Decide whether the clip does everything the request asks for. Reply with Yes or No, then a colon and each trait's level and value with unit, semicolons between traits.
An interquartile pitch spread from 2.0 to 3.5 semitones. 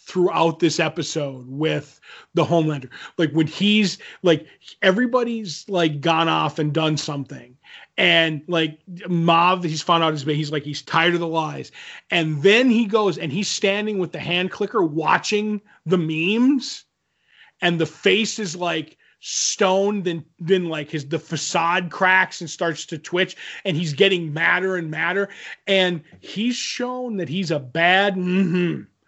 Yes: average, 3.2 semitones